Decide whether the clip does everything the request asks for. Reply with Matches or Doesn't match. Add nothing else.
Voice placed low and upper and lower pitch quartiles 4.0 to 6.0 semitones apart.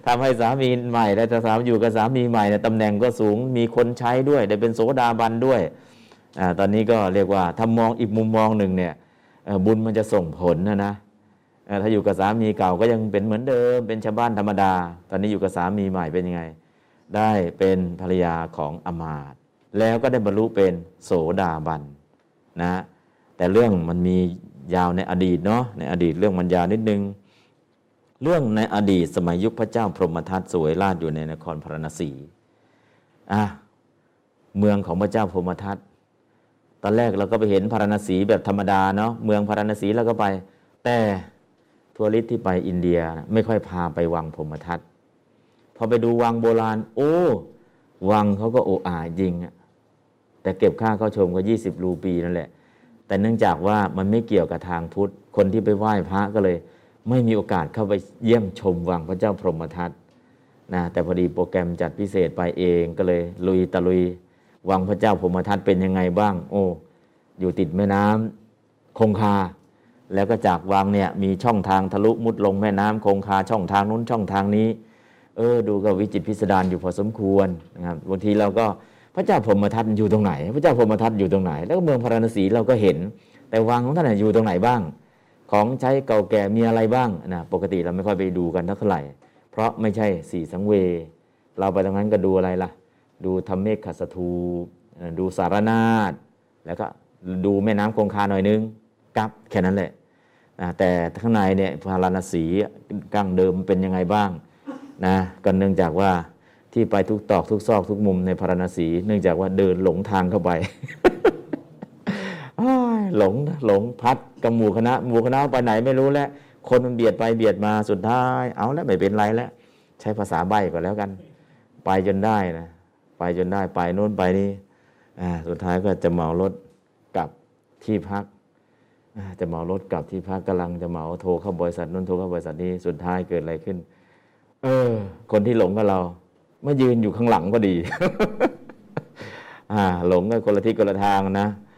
Doesn't match